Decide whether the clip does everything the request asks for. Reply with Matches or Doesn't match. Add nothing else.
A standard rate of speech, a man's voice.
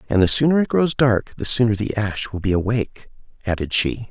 Doesn't match